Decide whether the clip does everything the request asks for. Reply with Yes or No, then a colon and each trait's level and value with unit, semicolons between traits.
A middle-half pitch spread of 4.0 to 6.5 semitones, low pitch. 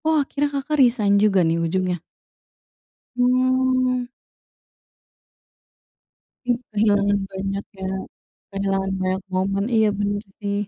No: average, 4.6 semitones; high, 205 Hz